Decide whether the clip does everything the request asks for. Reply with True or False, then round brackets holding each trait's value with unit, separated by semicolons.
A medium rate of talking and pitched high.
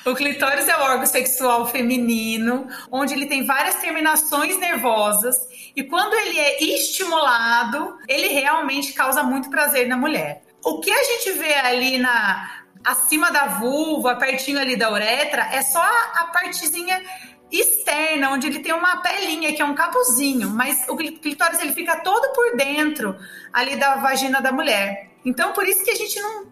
True (165 wpm; 285 Hz)